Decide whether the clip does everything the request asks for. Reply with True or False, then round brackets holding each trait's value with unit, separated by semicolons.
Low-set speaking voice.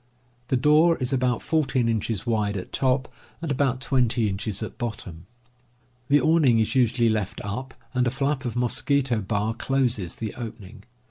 True (120 Hz)